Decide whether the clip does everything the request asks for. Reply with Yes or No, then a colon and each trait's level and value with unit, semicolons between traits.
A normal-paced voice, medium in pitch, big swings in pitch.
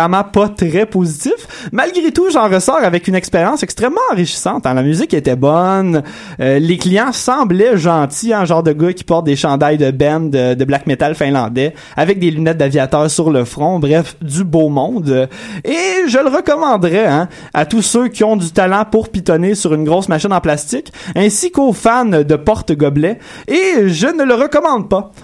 Yes: average, 190 wpm; medium, 175 Hz; wide, 6.1 semitones